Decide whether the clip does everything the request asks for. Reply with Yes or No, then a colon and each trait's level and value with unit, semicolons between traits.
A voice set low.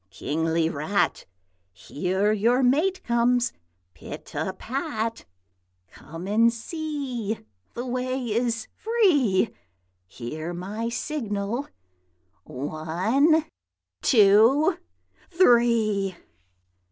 No: high, 230 Hz